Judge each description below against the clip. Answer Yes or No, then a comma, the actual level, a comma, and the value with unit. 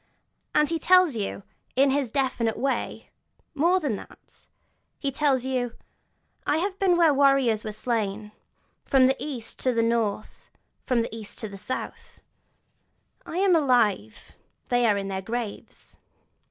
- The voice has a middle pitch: No, very high, 255 Hz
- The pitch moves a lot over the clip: No, average, 4.7 semitones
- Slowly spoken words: No, average, 155 wpm